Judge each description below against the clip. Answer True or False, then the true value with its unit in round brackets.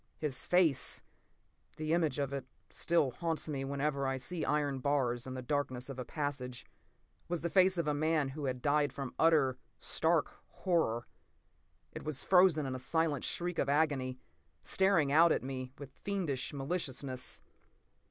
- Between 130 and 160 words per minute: True (155 wpm)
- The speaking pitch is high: False (145 Hz)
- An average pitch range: True (3.6 semitones)